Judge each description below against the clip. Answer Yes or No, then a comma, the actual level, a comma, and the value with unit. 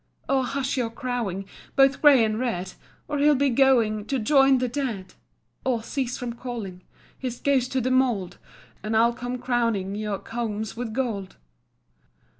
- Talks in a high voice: Yes, high, 240 Hz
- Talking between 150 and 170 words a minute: Yes, average, 160 wpm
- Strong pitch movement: No, average, 3.5 semitones